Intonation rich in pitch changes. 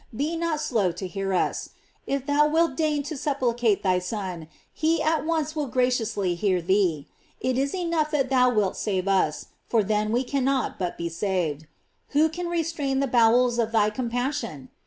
Yes: wide, 7.0 semitones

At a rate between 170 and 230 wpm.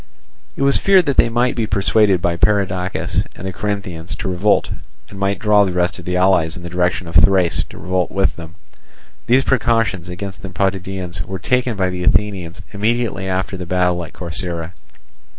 Yes: average, 185 wpm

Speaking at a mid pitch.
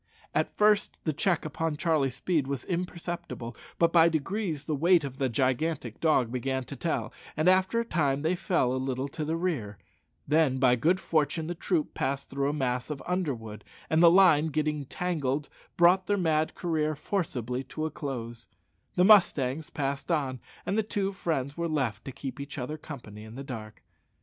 Yes: medium, 150 Hz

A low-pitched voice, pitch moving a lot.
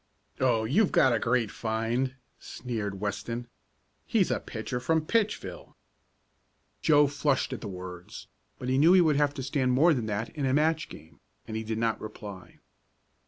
No: low, 125 Hz; average, 4.8 semitones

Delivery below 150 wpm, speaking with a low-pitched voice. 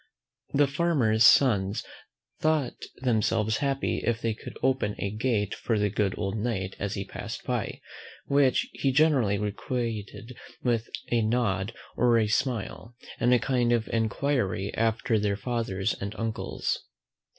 Yes: average, 140 wpm; low, 115 Hz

